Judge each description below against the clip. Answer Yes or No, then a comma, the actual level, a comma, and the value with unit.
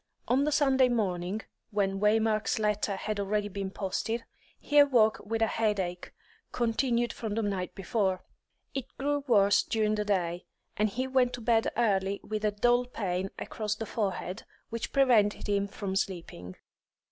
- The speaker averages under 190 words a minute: Yes, average, 160 wpm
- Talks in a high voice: Yes, high, 215 Hz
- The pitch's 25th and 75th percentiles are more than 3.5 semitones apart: No, average, 3.1 semitones